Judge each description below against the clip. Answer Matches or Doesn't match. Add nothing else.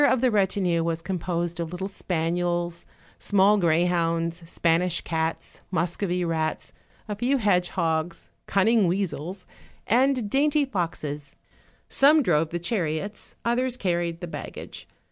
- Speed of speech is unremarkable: Doesn't match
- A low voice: Doesn't match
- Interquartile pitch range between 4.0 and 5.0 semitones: Doesn't match